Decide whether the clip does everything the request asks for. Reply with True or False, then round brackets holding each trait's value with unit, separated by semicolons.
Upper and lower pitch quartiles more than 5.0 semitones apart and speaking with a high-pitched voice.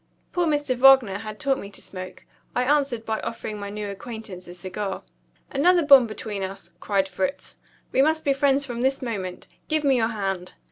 True (5.6 semitones; 230 Hz)